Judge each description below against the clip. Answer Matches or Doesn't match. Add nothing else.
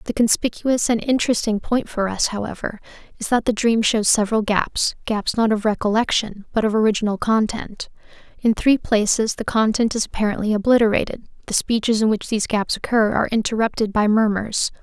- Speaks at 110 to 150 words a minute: Doesn't match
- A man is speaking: Doesn't match